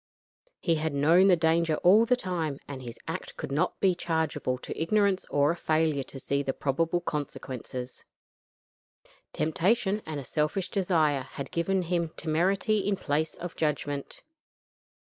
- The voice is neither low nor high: Yes, medium, 160 Hz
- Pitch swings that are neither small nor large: Yes, average, 4.2 semitones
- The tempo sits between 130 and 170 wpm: Yes, average, 145 wpm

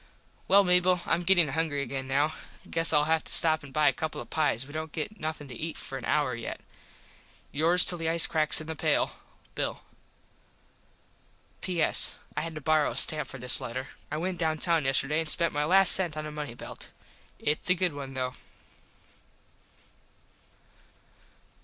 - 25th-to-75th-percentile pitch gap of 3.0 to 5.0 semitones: No, narrow, 2.5 semitones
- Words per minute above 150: Yes, average, 185 wpm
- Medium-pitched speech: Yes, medium, 155 Hz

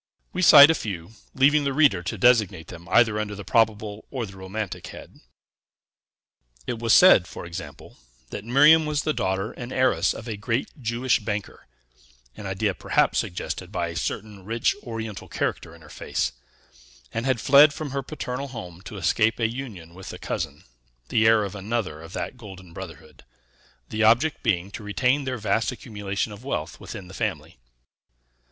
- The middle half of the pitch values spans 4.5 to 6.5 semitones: Yes, average, 4.8 semitones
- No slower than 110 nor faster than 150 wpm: No, average, 175 wpm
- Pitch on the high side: No, low, 110 Hz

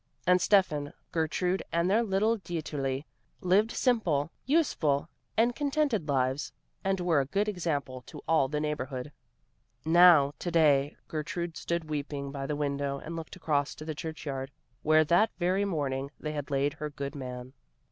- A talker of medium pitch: Yes, medium, 155 Hz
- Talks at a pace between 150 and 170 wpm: Yes, average, 160 wpm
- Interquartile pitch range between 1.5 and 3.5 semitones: No, average, 4.3 semitones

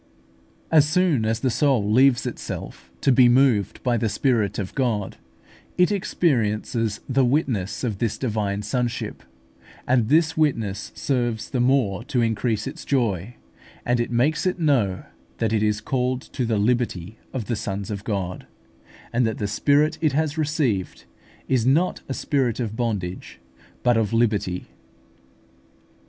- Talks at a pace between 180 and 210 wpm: No, average, 150 wpm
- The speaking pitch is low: Yes, low, 120 Hz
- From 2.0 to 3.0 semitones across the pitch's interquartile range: No, average, 4.3 semitones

